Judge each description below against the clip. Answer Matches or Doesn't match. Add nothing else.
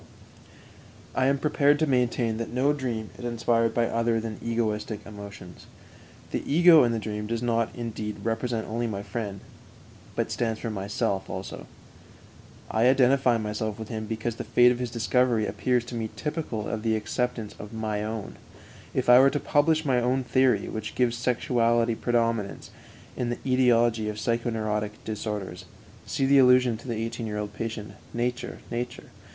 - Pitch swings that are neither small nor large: Doesn't match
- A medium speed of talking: Matches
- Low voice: Matches